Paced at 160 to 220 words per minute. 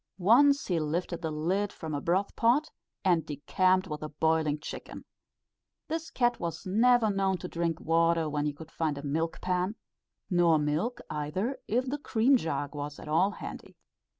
Yes: average, 175 wpm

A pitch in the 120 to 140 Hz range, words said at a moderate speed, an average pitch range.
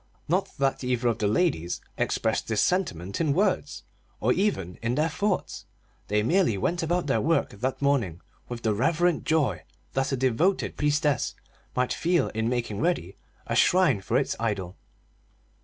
No: low, 135 Hz; average, 160 wpm; wide, 7.1 semitones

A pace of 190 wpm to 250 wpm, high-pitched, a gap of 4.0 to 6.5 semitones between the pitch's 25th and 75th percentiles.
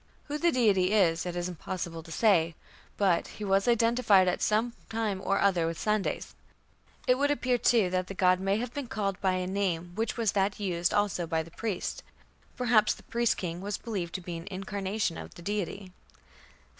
No: average, 195 wpm; high, 195 Hz; average, 3.5 semitones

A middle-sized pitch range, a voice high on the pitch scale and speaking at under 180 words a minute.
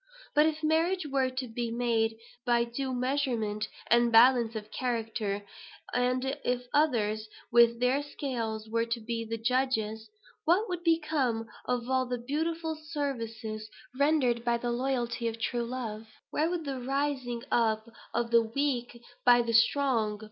Yes: average, 3.2 semitones; high, 245 Hz; average, 155 wpm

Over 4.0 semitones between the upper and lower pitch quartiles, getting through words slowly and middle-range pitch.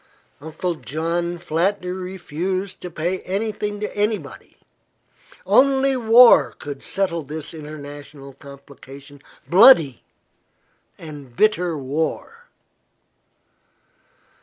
Yes: wide, 5.5 semitones; slow, 85 wpm; medium, 170 Hz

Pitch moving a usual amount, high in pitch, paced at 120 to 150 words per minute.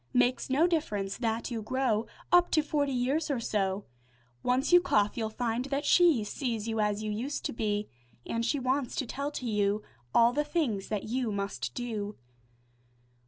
No: average, 4.7 semitones; high, 235 Hz; average, 180 wpm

